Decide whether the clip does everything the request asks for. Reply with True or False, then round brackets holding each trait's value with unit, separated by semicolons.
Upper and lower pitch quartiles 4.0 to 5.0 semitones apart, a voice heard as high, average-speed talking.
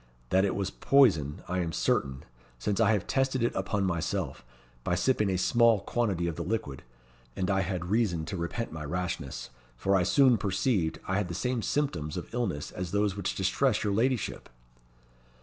False (4.7 semitones; 95 Hz; 185 wpm)